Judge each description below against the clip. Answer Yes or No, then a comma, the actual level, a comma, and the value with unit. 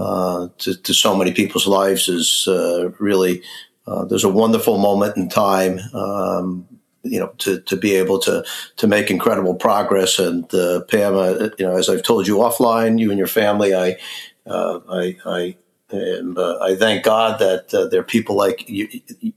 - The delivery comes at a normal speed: Yes, average, 190 wpm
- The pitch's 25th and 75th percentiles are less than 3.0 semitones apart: No, average, 3.4 semitones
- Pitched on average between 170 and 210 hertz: No, very low, 95 Hz